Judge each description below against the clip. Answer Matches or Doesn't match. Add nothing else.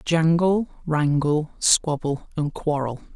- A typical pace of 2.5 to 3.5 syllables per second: Matches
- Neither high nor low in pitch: Matches